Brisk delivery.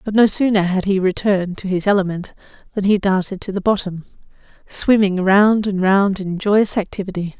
No: average, 180 wpm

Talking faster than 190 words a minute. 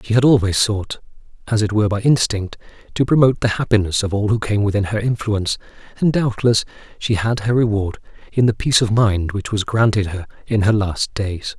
Yes: average, 200 wpm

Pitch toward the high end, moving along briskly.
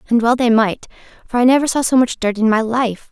Yes: high, 235 Hz; fast, 270 wpm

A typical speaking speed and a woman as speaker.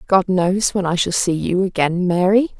No: fast, 210 wpm; female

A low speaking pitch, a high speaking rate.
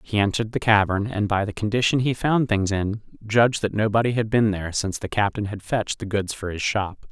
Yes: low, 105 Hz; fast, 235 wpm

